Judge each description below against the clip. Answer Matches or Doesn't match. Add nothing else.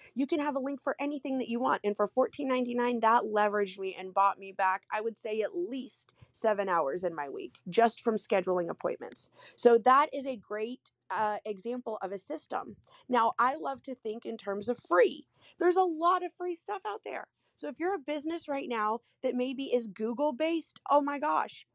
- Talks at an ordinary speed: Doesn't match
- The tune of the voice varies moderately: Doesn't match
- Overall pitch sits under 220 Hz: Doesn't match